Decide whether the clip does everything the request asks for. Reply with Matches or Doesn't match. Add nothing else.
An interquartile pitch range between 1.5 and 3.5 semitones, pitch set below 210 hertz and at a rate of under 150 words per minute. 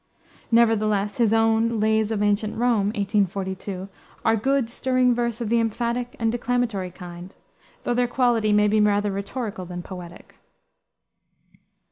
Doesn't match